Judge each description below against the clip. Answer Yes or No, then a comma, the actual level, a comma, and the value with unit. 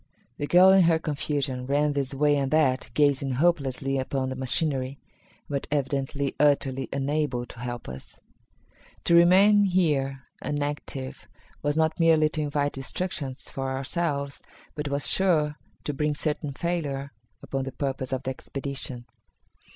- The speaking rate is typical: Yes, average, 145 wpm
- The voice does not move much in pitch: Yes, narrow, 2.3 semitones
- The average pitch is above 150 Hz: No, medium, 140 Hz